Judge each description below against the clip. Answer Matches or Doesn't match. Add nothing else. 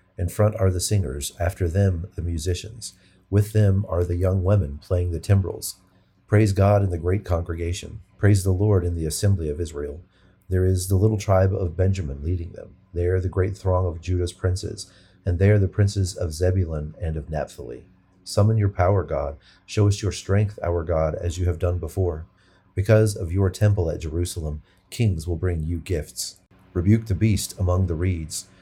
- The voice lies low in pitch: Matches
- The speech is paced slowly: Doesn't match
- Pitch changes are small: Matches